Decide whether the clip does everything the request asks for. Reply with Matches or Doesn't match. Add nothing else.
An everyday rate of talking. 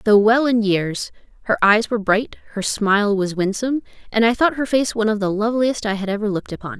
Doesn't match